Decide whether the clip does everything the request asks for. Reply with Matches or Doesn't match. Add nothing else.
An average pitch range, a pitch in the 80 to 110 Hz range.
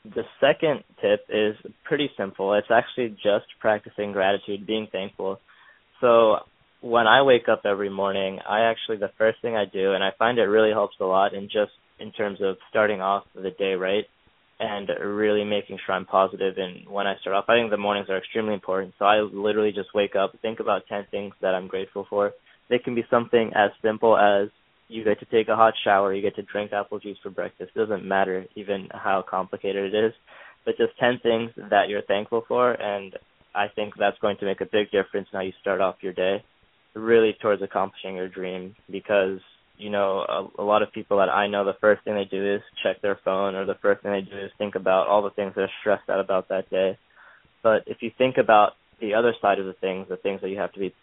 Doesn't match